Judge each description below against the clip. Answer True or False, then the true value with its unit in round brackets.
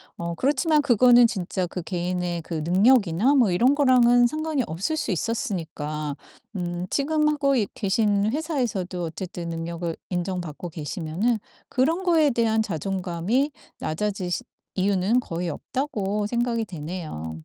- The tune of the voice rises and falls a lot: True (6.4 semitones)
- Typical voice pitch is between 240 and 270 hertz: False (200 Hz)